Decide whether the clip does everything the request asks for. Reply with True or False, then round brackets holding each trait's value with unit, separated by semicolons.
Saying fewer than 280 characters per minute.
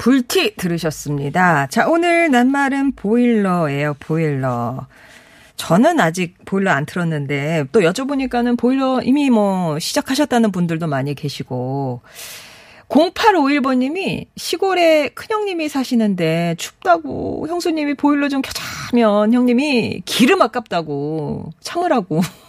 True (270 characters per minute)